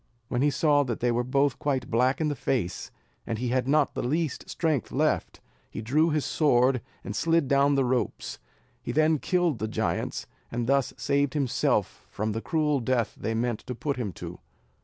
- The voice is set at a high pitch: No, low, 130 Hz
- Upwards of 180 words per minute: Yes, average, 190 wpm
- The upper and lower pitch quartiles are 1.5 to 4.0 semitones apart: Yes, average, 3.4 semitones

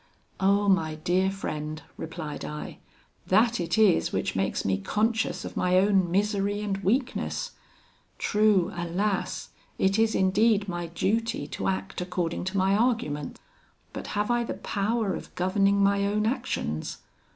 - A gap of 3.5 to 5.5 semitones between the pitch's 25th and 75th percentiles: No, average, 3.1 semitones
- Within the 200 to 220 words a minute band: No, average, 145 wpm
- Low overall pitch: No, high, 195 Hz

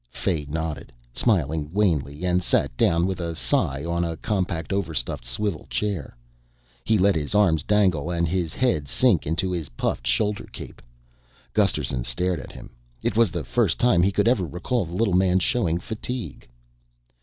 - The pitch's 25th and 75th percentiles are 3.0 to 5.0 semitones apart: Yes, average, 4.3 semitones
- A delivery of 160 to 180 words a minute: Yes, average, 165 wpm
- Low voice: Yes, very low, 90 Hz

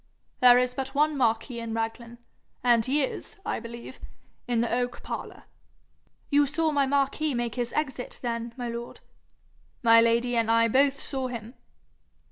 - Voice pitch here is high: Yes, high, 245 Hz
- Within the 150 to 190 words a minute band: Yes, average, 160 wpm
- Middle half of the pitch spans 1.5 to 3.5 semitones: Yes, narrow, 2.6 semitones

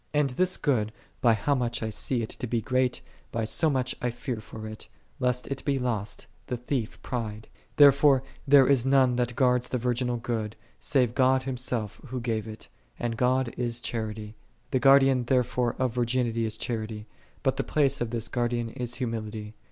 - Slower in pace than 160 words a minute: No, average, 185 wpm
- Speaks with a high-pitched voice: No, low, 125 Hz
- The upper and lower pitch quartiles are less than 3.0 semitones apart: Yes, narrow, 2.4 semitones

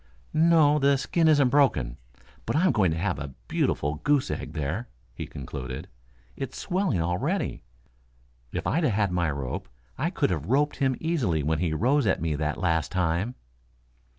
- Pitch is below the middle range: Yes, very low, 95 Hz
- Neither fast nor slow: Yes, average, 165 wpm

